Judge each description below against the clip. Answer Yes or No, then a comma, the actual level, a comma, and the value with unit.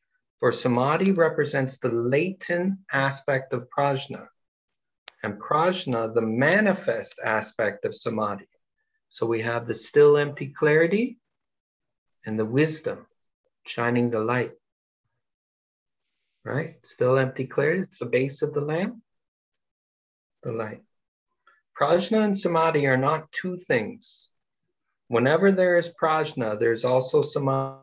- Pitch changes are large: Yes, wide, 6.3 semitones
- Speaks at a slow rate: Yes, slow, 115 wpm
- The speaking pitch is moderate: Yes, medium, 145 Hz